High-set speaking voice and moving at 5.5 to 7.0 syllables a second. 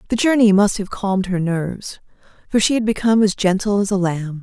Yes: high, 200 Hz; 5.9 syllables/s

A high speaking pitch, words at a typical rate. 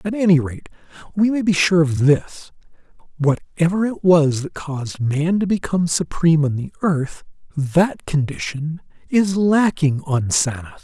No: medium, 165 Hz; average, 150 wpm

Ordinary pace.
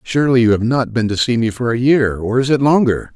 No: fast, 285 wpm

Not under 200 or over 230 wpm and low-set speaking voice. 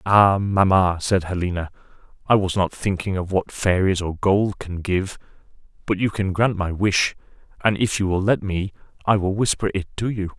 No: average, 190 wpm; very low, 95 Hz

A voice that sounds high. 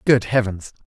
No: low, 110 Hz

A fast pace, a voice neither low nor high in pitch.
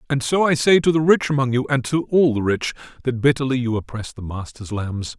No: fast, 245 wpm; low, 130 Hz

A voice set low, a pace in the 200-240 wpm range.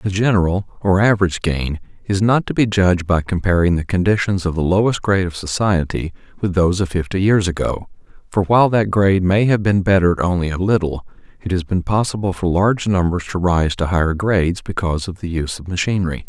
Yes: very low, 95 Hz; fast, 205 wpm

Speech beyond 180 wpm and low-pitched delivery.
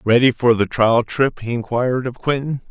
Yes: average, 200 wpm; low, 120 Hz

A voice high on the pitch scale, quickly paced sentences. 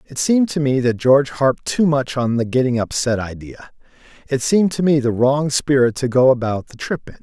No: low, 135 Hz; fast, 225 wpm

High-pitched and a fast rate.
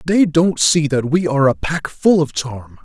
No: medium, 150 Hz; fast, 230 wpm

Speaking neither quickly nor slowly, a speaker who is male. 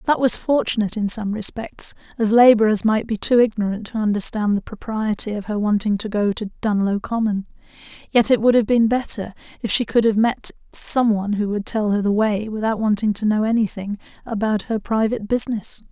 No: average, 195 wpm; female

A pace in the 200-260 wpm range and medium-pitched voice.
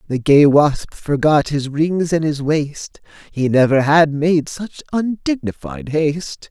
No: average, 145 wpm; medium, 150 Hz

